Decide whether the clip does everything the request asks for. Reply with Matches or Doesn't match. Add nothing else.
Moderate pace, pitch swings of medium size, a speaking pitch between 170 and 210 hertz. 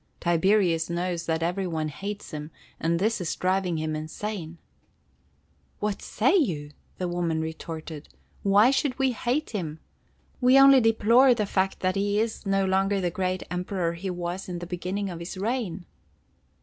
Matches